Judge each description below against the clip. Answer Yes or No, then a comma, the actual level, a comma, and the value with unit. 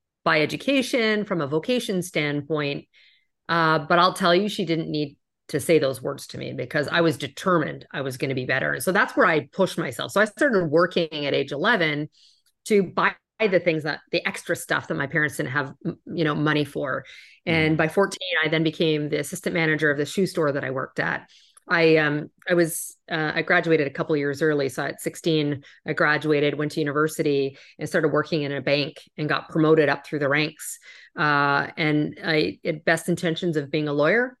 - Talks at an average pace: No, fast, 210 wpm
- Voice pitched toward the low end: No, medium, 160 Hz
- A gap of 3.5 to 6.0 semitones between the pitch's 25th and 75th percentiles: No, average, 2.9 semitones